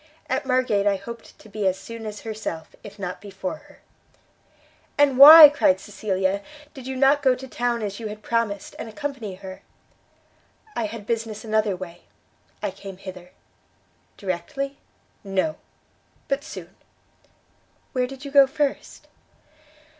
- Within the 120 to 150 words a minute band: Yes, average, 145 wpm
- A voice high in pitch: Yes, high, 220 Hz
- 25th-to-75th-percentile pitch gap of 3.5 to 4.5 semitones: No, average, 5.2 semitones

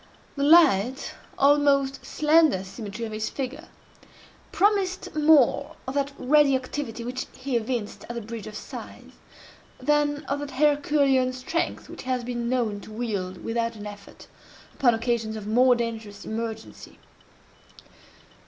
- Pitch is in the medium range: No, very high, 255 Hz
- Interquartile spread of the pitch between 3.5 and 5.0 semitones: Yes, average, 4.2 semitones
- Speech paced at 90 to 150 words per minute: Yes, average, 140 wpm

